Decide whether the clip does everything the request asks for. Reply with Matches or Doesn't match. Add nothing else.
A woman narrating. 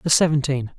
Doesn't match